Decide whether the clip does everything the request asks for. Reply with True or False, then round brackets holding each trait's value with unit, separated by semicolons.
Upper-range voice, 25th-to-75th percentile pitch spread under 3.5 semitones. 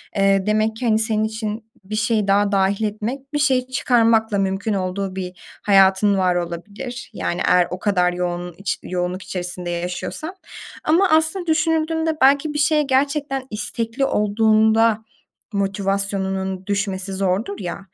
False (210 Hz; 4.5 semitones)